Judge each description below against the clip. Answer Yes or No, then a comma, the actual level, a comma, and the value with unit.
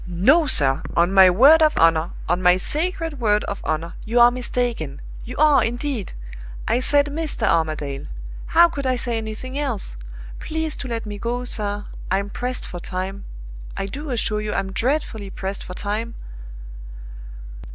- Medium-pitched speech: No, high, 225 Hz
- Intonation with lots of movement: Yes, wide, 6.0 semitones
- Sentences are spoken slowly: No, average, 160 wpm